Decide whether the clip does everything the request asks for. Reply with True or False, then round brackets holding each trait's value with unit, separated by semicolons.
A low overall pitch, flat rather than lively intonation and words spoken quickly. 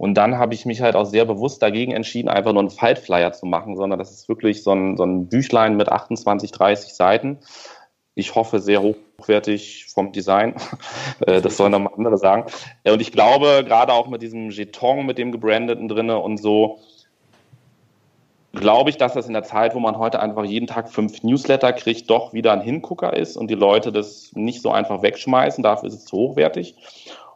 True (110 Hz; 2.3 semitones; 195 wpm)